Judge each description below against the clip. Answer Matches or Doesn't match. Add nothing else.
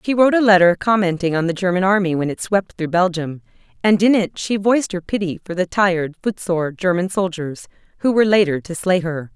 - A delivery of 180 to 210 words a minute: Matches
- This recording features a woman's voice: Matches